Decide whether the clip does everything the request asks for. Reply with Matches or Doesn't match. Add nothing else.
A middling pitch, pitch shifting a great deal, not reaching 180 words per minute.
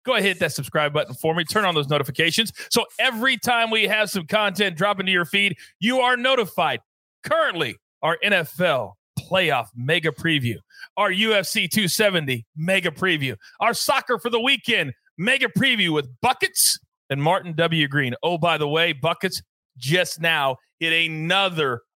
Matches